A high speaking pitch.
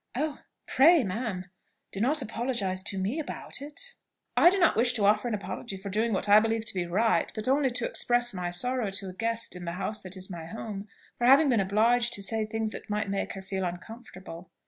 Yes: high, 215 Hz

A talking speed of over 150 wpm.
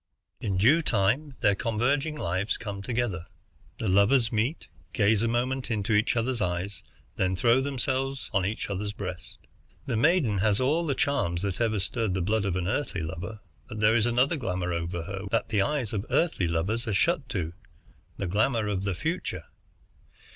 Yes: average, 185 wpm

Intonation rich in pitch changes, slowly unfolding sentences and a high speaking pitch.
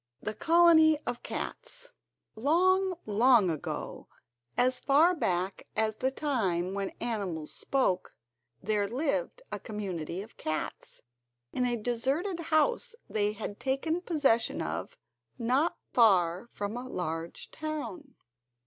Yes: wide, 7.5 semitones; slow, 120 wpm; high, 240 Hz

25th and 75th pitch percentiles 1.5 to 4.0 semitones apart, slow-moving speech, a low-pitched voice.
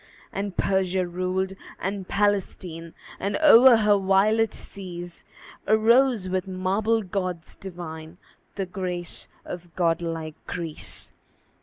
No: narrow, 2.6 semitones; slow, 110 wpm; medium, 185 Hz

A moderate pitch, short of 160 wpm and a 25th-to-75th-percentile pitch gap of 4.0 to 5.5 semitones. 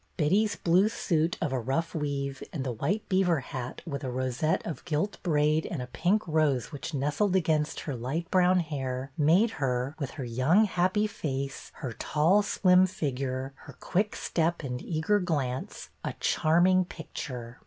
No: medium, 155 Hz; average, 165 wpm; average, 5.1 semitones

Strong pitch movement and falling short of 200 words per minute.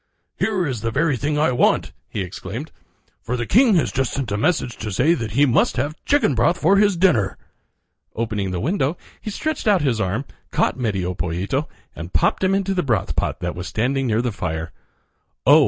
No: wide, 8.4 semitones; fast, 205 wpm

